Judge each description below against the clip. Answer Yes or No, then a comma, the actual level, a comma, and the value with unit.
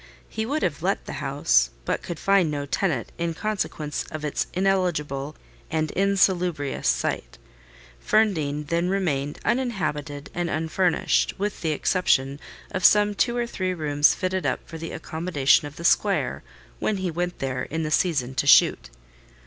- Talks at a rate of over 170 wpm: No, average, 155 wpm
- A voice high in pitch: No, medium, 165 Hz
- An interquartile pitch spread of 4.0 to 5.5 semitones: Yes, average, 4.6 semitones